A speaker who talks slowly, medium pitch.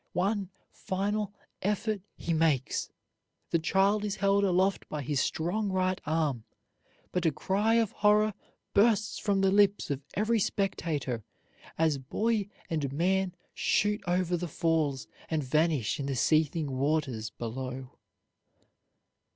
Yes: slow, 130 wpm; medium, 175 Hz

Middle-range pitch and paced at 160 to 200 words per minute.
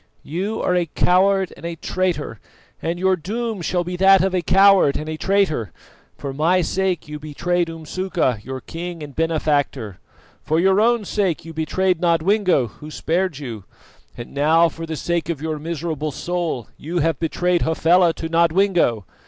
Yes: medium, 170 Hz; average, 170 wpm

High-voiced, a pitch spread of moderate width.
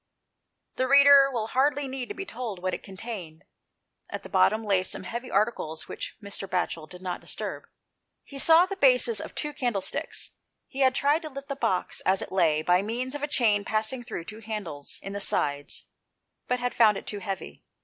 No: high, 220 Hz; wide, 5.9 semitones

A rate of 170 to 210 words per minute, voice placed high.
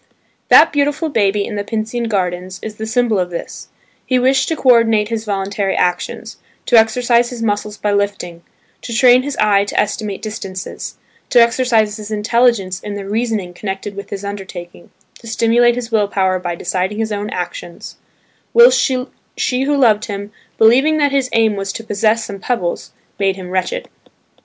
Yes: average, 175 wpm; high, 215 Hz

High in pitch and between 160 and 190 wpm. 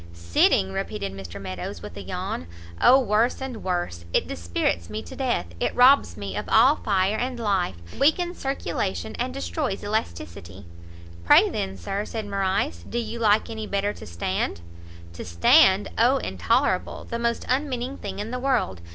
Yes: high, 200 Hz; average, 170 wpm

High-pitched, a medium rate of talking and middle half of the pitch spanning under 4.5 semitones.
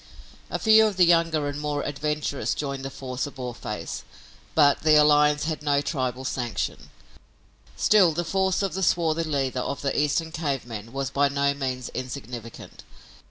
No: medium, 145 Hz; average, 165 wpm; average, 3.2 semitones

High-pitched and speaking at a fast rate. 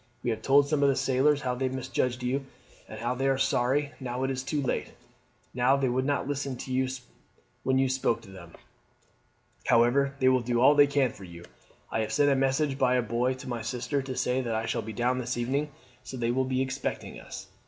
No: low, 130 Hz; fast, 220 wpm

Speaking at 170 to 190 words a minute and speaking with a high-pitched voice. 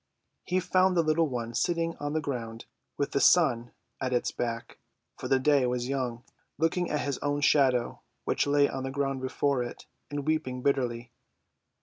No: average, 180 wpm; medium, 140 Hz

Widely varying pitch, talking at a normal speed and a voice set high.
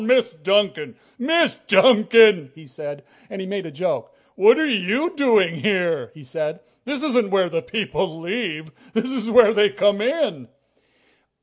Yes: wide, 6.7 semitones; average, 165 wpm; high, 205 Hz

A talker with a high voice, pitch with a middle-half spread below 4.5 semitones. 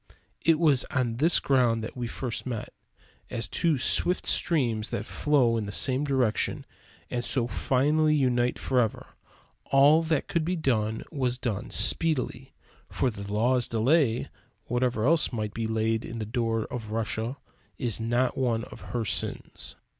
No: low, 125 Hz; average, 3.5 semitones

